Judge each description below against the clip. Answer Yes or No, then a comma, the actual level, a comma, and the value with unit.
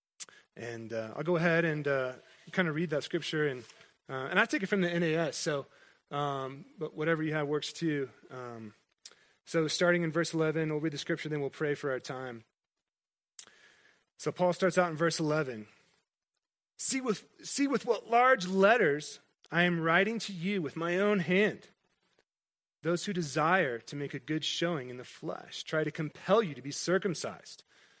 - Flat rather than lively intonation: No, average, 3.9 semitones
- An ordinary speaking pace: Yes, average, 185 wpm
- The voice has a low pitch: No, medium, 160 Hz